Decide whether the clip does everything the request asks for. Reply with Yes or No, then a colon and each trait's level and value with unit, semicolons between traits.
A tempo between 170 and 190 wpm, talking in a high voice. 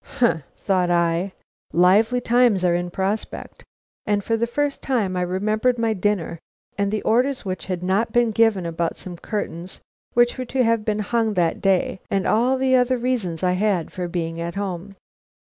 Yes: average, 180 wpm; high, 205 Hz